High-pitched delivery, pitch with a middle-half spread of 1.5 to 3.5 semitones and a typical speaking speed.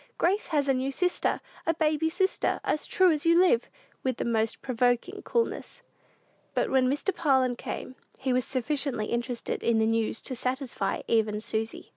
No: very high, 265 Hz; average, 5.3 semitones; average, 170 wpm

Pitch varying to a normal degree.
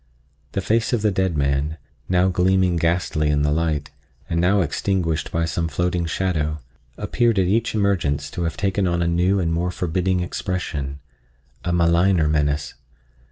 Yes: average, 3.3 semitones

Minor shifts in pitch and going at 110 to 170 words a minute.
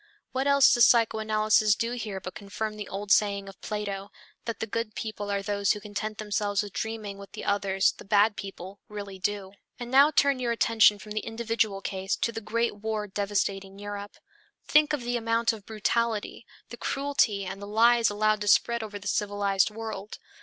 No: narrow, 2.2 semitones; average, 190 wpm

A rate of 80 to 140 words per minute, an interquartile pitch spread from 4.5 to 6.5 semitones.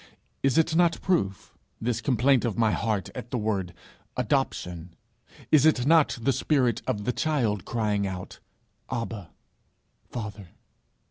Yes: slow, 135 wpm; average, 5.0 semitones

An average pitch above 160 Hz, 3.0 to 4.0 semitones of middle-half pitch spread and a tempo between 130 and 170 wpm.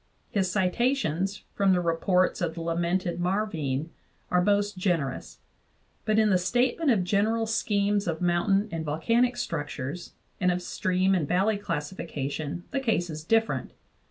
Yes: medium, 185 Hz; average, 3.7 semitones; average, 145 wpm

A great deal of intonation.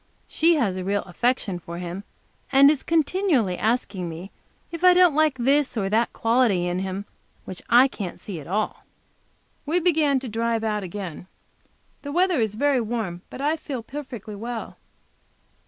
Yes: wide, 6.8 semitones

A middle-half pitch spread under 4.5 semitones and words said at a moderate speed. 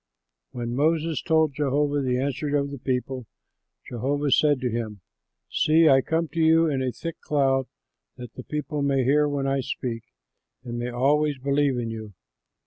Yes: average, 2.9 semitones; average, 170 wpm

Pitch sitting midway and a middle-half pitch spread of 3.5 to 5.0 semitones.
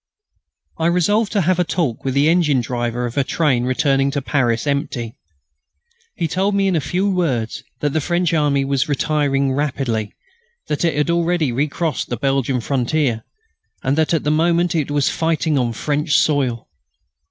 Yes: medium, 145 Hz; average, 4.0 semitones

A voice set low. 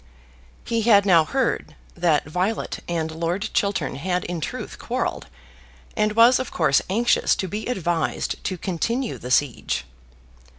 No: medium, 185 Hz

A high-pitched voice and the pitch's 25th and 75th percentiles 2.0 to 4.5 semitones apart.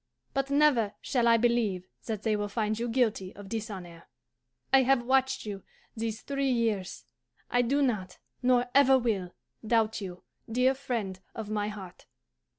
Yes: high, 225 Hz; average, 3.7 semitones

